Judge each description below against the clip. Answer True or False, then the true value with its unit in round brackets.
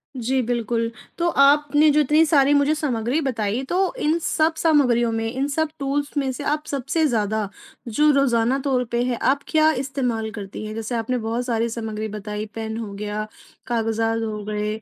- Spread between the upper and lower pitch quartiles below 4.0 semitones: False (4.3 semitones)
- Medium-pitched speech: False (245 Hz)